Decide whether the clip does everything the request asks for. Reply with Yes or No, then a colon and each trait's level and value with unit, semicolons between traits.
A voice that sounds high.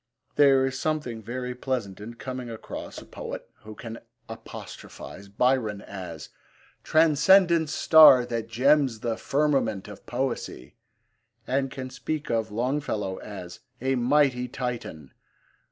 No: low, 125 Hz